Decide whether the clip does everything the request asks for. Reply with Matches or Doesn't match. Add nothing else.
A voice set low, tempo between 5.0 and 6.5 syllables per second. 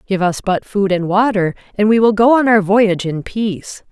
Doesn't match